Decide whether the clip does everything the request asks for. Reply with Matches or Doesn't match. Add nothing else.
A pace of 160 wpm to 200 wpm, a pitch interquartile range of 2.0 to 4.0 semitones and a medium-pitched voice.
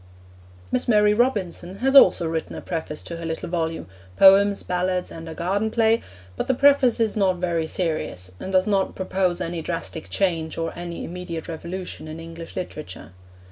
Matches